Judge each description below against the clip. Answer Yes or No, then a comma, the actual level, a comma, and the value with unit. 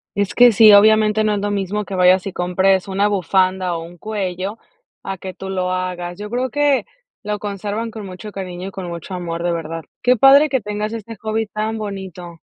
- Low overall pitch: No, high, 200 Hz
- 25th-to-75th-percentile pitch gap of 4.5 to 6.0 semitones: No, average, 2.8 semitones